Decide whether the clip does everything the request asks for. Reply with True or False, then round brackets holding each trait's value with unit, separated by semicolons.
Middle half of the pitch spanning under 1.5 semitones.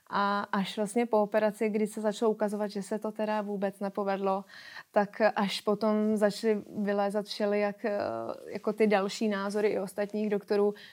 True (1.1 semitones)